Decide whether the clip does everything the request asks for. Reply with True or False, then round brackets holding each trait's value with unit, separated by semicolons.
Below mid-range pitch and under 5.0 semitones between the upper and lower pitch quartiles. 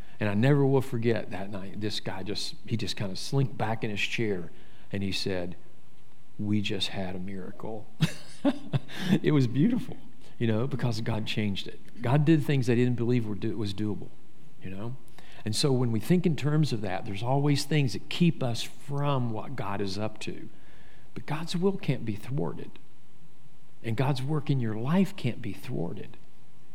False (120 Hz; 5.4 semitones)